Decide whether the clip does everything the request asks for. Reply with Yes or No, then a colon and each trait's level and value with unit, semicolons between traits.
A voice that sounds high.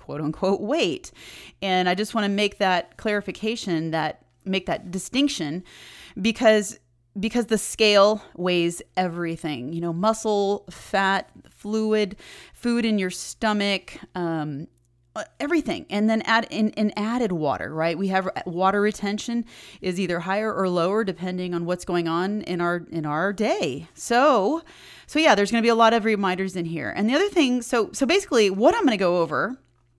Yes: high, 195 Hz